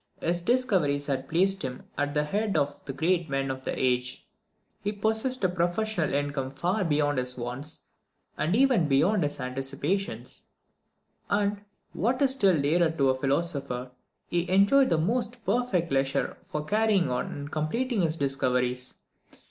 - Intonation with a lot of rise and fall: Yes, wide, 6.6 semitones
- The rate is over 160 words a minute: No, average, 155 wpm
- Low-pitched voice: No, medium, 160 Hz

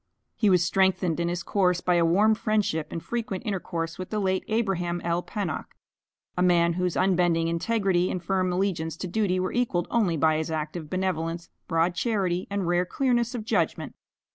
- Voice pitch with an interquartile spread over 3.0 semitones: No, average, 2.7 semitones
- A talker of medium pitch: Yes, medium, 180 Hz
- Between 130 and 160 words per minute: No, average, 180 wpm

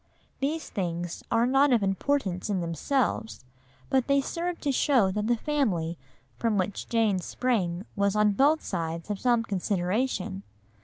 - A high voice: Yes, high, 210 Hz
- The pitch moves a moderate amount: No, wide, 6.1 semitones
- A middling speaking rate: Yes, average, 150 wpm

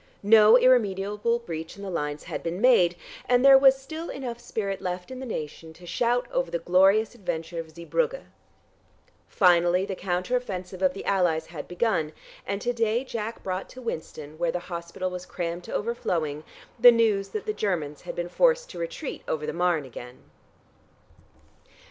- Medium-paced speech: Yes, average, 175 wpm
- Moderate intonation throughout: No, wide, 5.7 semitones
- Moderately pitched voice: No, high, 195 Hz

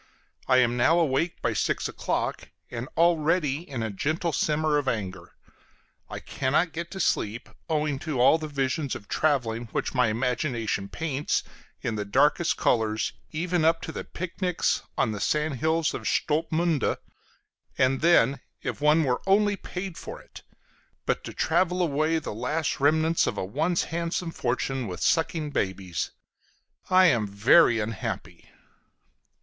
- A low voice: No, medium, 150 Hz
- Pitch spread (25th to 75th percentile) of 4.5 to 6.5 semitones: Yes, wide, 5.4 semitones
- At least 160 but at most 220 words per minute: No, average, 150 wpm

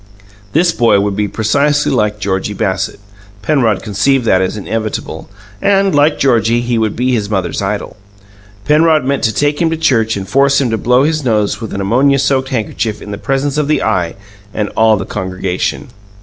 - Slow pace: No, average, 190 wpm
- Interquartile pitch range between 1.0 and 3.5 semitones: No, average, 5.3 semitones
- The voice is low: Yes, low, 115 Hz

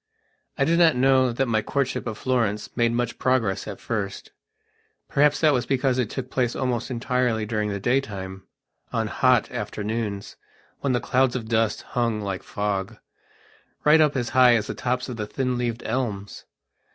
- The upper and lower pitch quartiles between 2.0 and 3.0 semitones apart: No, average, 3.4 semitones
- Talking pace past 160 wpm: Yes, average, 175 wpm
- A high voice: No, low, 120 Hz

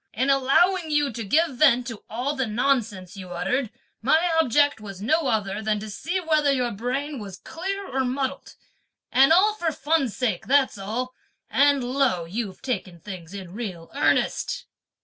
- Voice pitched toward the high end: Yes, very high, 250 Hz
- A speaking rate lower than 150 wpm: No, average, 170 wpm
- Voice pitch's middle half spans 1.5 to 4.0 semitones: No, wide, 5.5 semitones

